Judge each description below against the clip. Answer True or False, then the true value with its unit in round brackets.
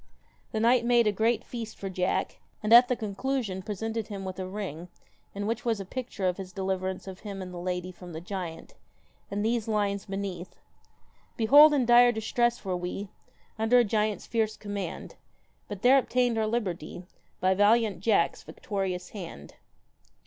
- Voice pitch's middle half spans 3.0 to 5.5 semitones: True (3.5 semitones)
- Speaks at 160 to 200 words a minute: True (175 wpm)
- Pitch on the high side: True (205 Hz)